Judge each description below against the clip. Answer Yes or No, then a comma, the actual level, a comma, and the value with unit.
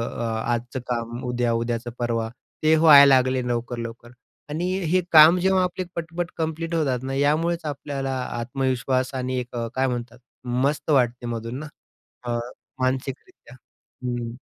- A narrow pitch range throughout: No, average, 4.2 semitones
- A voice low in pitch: Yes, low, 130 Hz